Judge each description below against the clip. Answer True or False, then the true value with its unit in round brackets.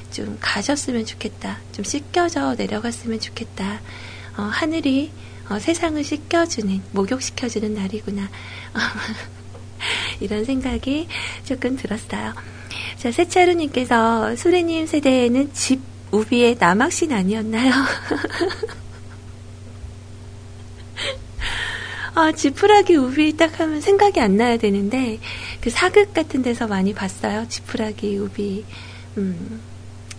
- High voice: True (215 Hz)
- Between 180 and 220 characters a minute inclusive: False (235 characters per minute)